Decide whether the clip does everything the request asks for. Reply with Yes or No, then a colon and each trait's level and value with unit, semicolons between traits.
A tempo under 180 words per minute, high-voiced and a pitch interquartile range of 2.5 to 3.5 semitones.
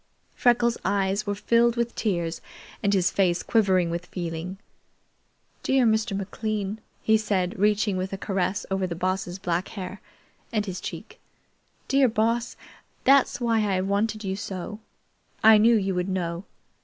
Yes: average, 150 wpm; high, 200 Hz; average, 2.9 semitones